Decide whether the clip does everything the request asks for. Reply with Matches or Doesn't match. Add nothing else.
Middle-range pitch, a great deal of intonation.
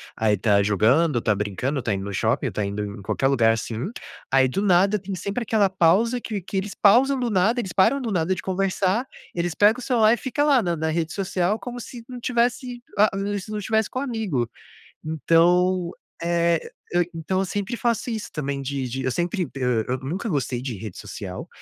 Matches